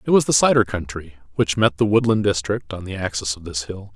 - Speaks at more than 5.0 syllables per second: Yes, 5.8 syllables/s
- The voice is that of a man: Yes, male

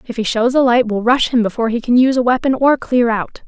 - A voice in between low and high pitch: No, high, 240 Hz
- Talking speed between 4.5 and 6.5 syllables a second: Yes, 6.4 syllables/s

